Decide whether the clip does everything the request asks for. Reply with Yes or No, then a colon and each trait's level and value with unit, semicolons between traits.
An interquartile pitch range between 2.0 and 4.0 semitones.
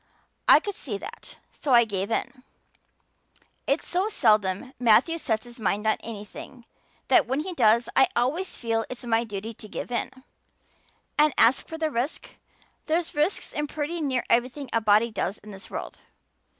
No: average, 5.3 semitones